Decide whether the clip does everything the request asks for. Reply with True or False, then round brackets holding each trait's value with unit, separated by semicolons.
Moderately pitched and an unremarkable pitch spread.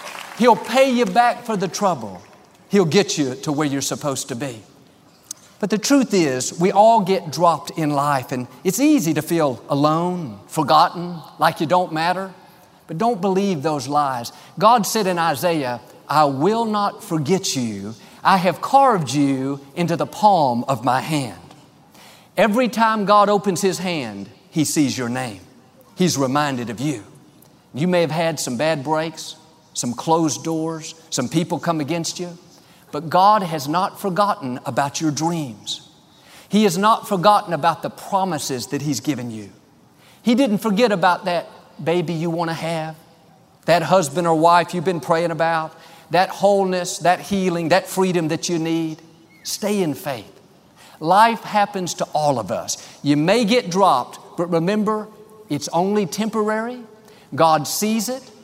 True (170 Hz; 4.6 semitones)